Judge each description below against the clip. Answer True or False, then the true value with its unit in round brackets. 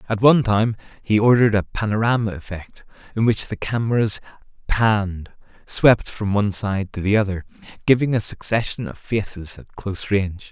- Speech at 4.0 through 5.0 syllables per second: False (5.4 syllables/s)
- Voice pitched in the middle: False (105 Hz)